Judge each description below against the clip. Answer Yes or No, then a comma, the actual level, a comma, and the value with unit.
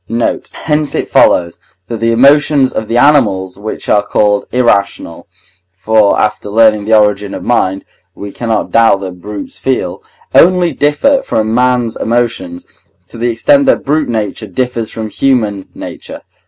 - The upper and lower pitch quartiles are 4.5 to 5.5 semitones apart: No, average, 3.8 semitones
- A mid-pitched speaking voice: No, low, 115 Hz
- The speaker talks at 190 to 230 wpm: No, average, 155 wpm